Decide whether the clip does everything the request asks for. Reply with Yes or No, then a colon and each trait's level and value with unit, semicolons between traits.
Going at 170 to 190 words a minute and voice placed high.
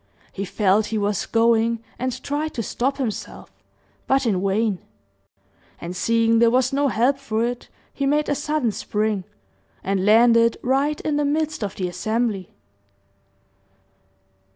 No: average, 145 wpm; high, 230 Hz